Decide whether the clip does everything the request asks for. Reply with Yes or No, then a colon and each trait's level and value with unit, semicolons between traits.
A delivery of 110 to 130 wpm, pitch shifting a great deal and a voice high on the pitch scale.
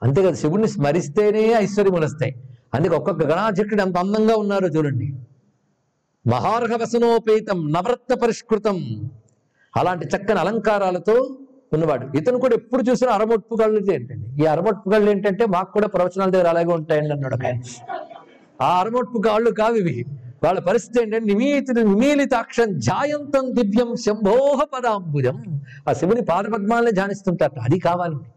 Yes: average, 115 wpm; wide, 6.7 semitones; high, 200 Hz